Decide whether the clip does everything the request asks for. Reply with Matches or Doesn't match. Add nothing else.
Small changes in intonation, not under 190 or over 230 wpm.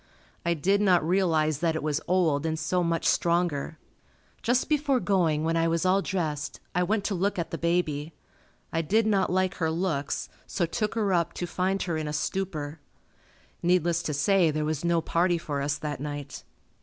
Doesn't match